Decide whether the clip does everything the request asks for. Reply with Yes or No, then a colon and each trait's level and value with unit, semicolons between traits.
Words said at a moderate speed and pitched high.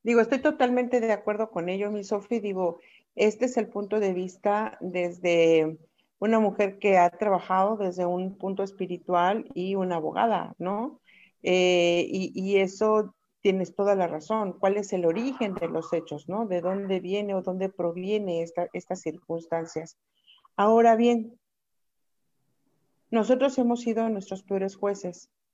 Yes: average, 150 wpm; high, 195 Hz